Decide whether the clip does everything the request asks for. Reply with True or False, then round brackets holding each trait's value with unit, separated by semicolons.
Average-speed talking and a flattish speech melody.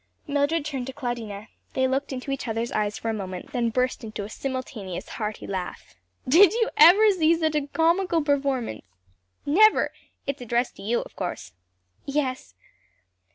False (160 wpm; 5.1 semitones)